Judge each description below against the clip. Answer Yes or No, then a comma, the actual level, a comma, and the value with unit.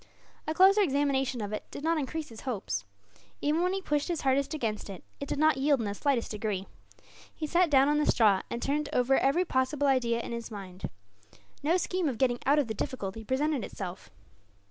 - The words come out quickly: Yes, fast, 210 wpm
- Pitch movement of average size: Yes, average, 4.9 semitones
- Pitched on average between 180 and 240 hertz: No, very high, 270 Hz